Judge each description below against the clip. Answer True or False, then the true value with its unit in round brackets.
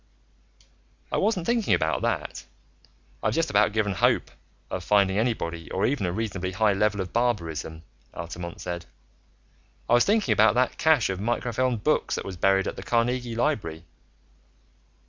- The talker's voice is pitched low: True (105 Hz)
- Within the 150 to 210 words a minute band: True (160 wpm)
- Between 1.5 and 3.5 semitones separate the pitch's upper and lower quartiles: False (5.0 semitones)